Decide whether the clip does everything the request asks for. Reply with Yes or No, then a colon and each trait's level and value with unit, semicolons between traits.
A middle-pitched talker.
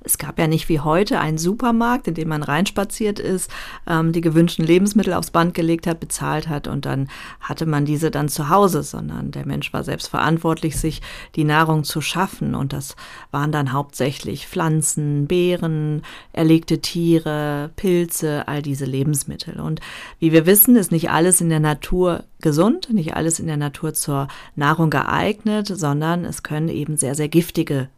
Yes: medium, 160 Hz